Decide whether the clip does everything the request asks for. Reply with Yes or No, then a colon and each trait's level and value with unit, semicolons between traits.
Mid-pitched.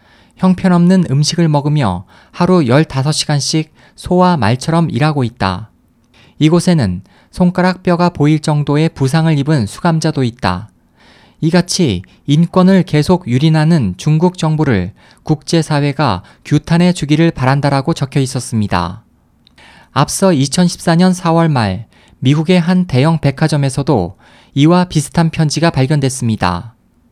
Yes: medium, 150 Hz